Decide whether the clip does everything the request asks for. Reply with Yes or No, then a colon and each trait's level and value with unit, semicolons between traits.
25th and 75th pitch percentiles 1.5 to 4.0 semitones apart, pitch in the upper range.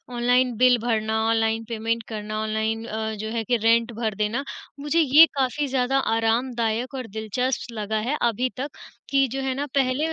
Yes: average, 2.8 semitones; high, 235 Hz